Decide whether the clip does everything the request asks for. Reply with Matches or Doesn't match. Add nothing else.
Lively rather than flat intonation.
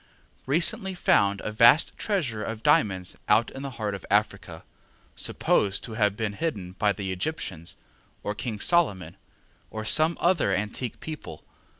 Matches